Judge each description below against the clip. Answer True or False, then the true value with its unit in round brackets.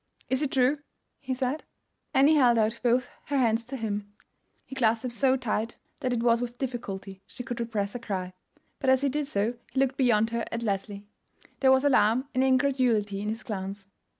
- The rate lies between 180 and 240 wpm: True (200 wpm)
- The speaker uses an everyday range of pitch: True (3.5 semitones)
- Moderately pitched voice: False (240 Hz)